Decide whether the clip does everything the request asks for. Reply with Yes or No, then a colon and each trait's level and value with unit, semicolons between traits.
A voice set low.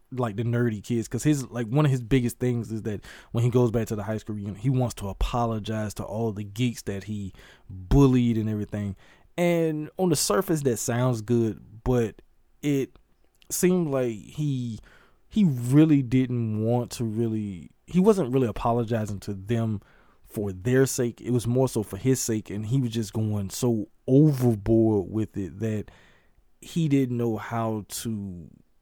Yes: low, 120 Hz